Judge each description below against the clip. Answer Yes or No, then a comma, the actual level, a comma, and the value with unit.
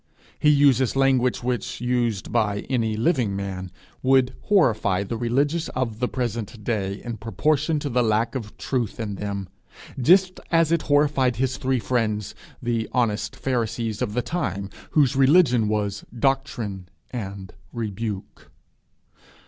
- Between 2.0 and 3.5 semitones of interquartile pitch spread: No, average, 4.0 semitones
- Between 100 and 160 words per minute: Yes, average, 140 wpm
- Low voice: Yes, low, 120 Hz